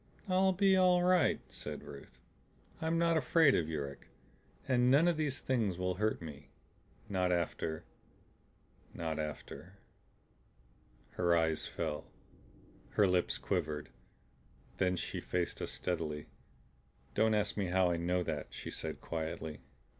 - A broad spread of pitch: Yes, wide, 8.7 semitones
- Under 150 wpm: Yes, slow, 135 wpm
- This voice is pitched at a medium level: No, very low, 90 Hz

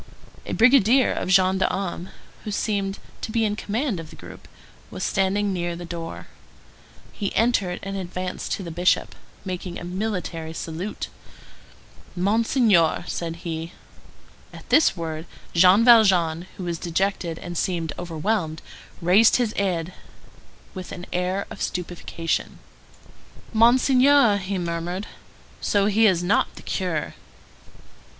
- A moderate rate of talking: No, slow, 130 wpm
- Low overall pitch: No, medium, 185 Hz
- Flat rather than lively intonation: No, average, 3.3 semitones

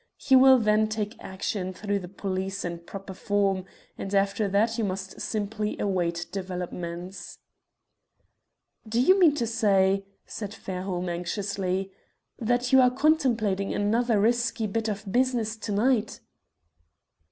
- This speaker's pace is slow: Yes, slow, 130 wpm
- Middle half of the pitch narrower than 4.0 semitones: Yes, average, 3.1 semitones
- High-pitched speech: Yes, high, 205 Hz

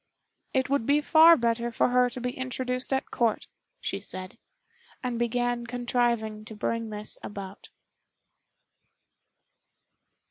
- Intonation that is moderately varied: No, narrow, 2.2 semitones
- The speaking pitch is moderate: No, high, 240 Hz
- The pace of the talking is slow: Yes, slow, 120 wpm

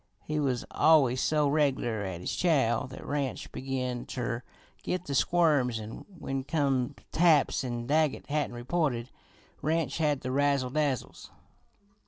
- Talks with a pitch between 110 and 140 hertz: Yes, low, 135 Hz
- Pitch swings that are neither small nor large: Yes, average, 3.5 semitones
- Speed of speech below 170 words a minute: Yes, average, 145 wpm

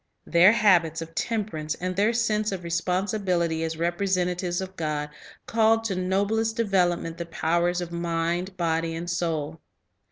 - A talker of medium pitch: Yes, medium, 175 Hz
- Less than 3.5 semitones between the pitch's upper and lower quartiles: Yes, average, 3.1 semitones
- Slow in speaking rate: No, average, 155 wpm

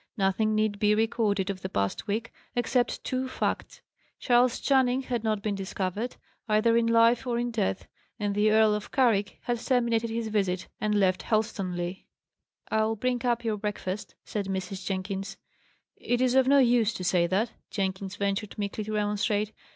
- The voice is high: Yes, high, 215 Hz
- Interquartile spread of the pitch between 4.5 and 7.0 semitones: No, average, 3.1 semitones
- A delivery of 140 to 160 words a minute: No, average, 170 wpm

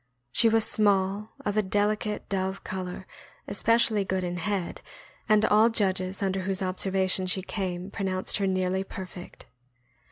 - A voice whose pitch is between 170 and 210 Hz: Yes, high, 190 Hz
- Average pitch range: No, narrow, 1.8 semitones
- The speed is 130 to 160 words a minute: Yes, average, 140 wpm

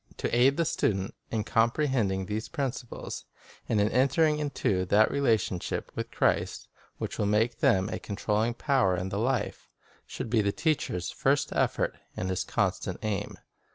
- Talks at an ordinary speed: Yes, average, 160 wpm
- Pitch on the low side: Yes, low, 110 Hz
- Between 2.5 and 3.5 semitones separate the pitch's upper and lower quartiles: No, average, 4.8 semitones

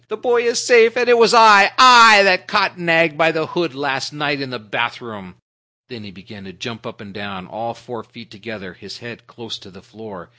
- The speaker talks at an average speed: No, fast, 225 wpm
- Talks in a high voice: No, low, 125 Hz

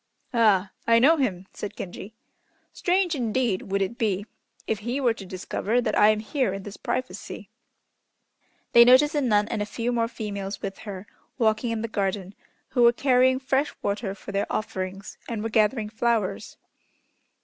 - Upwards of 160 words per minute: Yes, average, 170 wpm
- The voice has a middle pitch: No, high, 220 Hz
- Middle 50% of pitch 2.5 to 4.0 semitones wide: Yes, average, 3.6 semitones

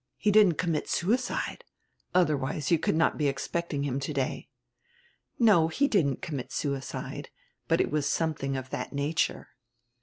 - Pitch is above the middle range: No, medium, 155 Hz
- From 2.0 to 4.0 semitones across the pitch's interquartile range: Yes, average, 3.6 semitones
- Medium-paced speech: Yes, average, 145 wpm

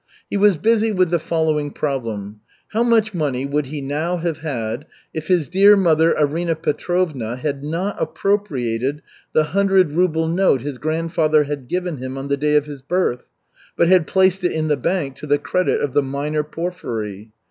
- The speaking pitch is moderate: Yes, medium, 155 Hz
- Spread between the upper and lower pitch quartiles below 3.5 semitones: No, average, 4.3 semitones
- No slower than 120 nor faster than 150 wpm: No, average, 180 wpm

